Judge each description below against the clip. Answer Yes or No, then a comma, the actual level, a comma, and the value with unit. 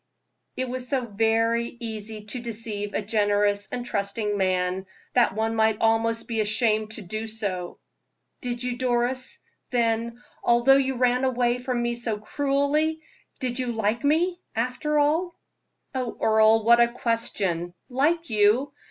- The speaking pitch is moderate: No, high, 235 Hz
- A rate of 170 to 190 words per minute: No, average, 145 wpm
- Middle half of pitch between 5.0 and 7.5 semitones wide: No, average, 2.8 semitones